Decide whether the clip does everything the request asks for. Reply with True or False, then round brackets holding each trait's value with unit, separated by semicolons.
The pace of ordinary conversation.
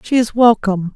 True (190 wpm)